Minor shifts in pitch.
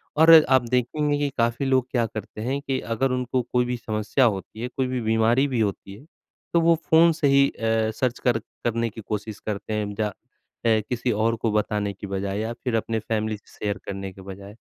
No: average, 3.4 semitones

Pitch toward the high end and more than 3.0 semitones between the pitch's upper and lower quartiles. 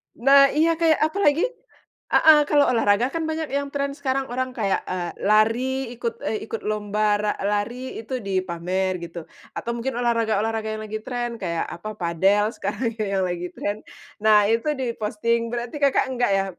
Yes: high, 225 Hz; average, 4.2 semitones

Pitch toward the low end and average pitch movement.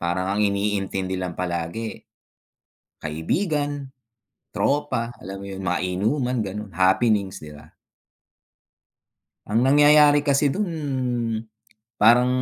No: low, 105 Hz; wide, 6.6 semitones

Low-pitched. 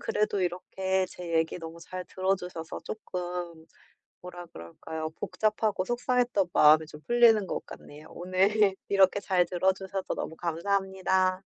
No: medium, 185 Hz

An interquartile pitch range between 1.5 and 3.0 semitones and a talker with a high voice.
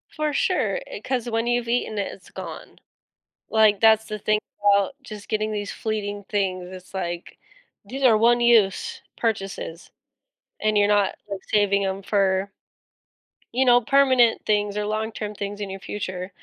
Yes: average, 2.7 semitones; high, 210 Hz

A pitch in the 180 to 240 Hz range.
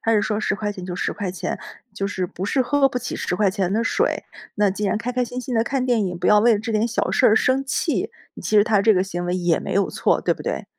Yes: high, 210 Hz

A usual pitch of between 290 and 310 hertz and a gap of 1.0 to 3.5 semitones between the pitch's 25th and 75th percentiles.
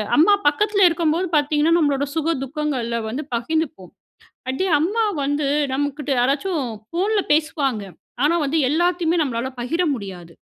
No: very high, 300 Hz; average, 3.9 semitones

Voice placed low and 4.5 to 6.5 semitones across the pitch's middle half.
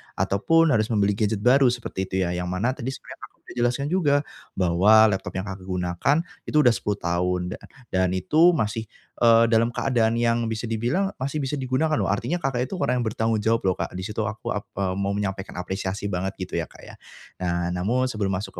Yes: low, 110 Hz; average, 4.8 semitones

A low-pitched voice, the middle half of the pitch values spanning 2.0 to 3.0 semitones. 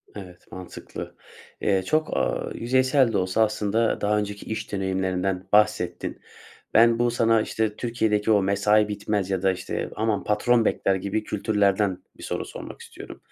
Yes: low, 105 Hz; narrow, 2.6 semitones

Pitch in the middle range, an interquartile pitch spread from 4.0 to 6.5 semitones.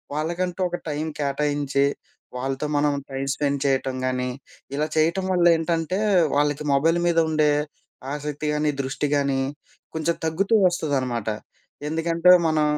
No: medium, 150 Hz; average, 3.0 semitones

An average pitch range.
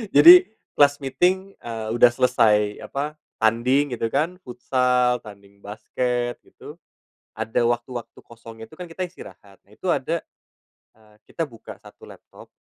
Yes: average, 3.0 semitones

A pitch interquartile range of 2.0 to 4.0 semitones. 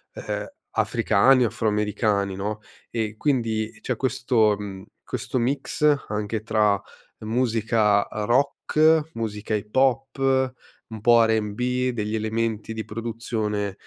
Yes: average, 2.9 semitones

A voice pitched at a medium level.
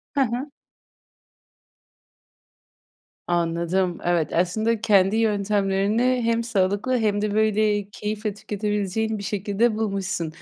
No: high, 205 Hz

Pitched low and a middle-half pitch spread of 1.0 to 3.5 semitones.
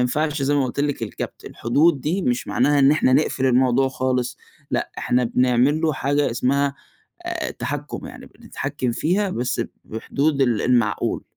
Yes: low, 130 Hz; average, 2.8 semitones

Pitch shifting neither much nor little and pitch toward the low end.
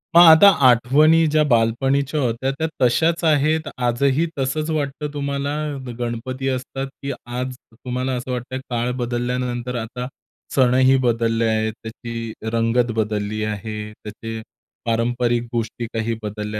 Yes: average, 3.1 semitones; low, 125 Hz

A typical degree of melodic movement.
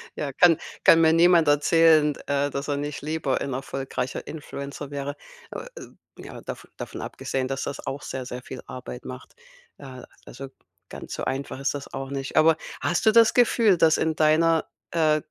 Yes: average, 3.0 semitones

